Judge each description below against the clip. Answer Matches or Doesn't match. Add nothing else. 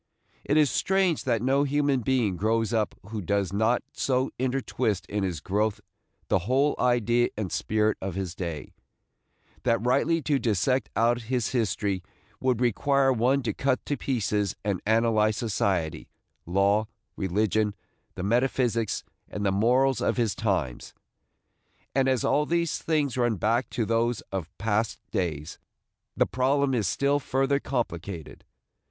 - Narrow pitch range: Doesn't match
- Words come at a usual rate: Matches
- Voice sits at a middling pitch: Doesn't match